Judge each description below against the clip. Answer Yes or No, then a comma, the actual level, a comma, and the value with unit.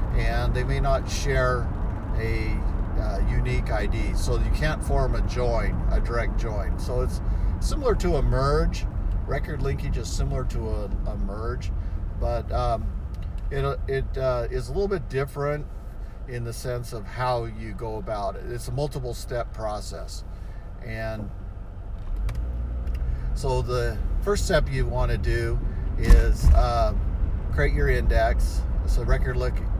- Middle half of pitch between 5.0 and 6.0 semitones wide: Yes, wide, 5.5 semitones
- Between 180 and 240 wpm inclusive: No, average, 145 wpm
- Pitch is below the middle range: Yes, low, 100 Hz